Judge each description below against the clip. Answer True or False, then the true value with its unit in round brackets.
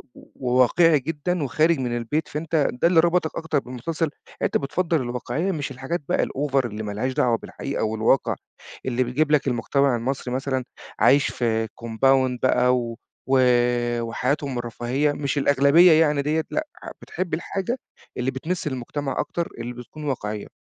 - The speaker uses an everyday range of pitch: True (4.1 semitones)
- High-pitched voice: False (135 Hz)